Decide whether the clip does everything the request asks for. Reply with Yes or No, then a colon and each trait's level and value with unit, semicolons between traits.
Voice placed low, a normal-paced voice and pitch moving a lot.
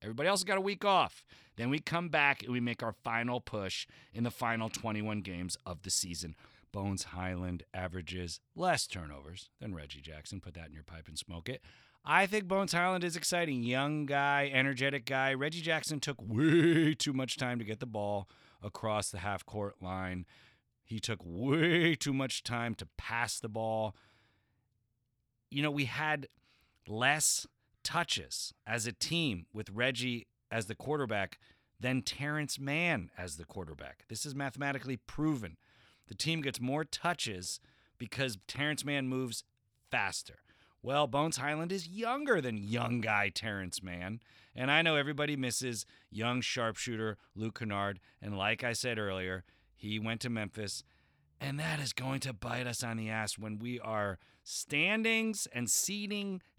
Yes: low, 120 Hz; average, 165 wpm; wide, 5.8 semitones